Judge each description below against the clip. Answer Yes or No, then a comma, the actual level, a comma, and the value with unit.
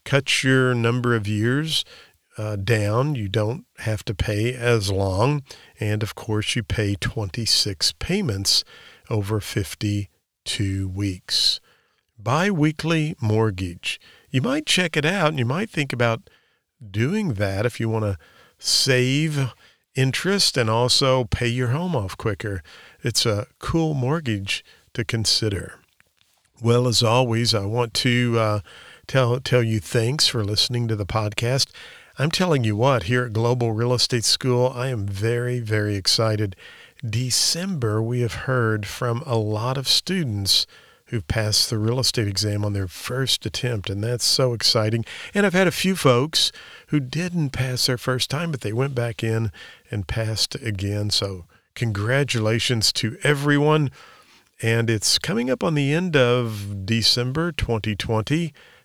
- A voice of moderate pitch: No, low, 120 Hz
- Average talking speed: Yes, average, 150 wpm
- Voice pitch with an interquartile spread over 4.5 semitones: No, average, 3.5 semitones